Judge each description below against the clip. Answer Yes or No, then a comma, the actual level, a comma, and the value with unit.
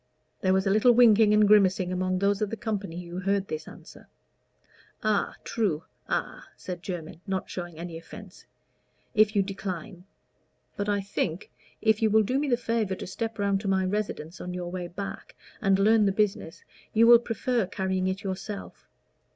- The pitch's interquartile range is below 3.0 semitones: Yes, narrow, 2.6 semitones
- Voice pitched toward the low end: No, high, 195 Hz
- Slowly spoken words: No, average, 180 wpm